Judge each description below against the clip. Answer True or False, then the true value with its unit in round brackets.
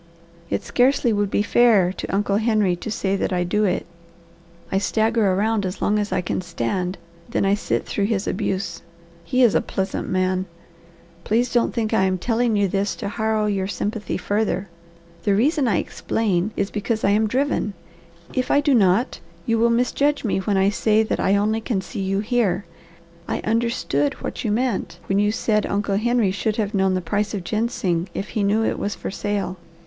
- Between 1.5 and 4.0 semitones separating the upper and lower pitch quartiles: True (2.7 semitones)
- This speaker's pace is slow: False (195 wpm)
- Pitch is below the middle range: False (205 Hz)